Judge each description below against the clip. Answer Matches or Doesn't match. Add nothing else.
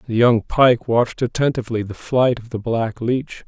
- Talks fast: Doesn't match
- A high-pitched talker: Doesn't match